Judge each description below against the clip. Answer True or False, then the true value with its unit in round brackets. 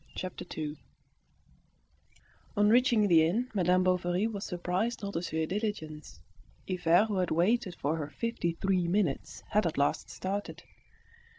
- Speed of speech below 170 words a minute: True (150 wpm)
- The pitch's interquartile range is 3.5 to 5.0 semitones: True (3.8 semitones)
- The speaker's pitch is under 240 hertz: True (185 Hz)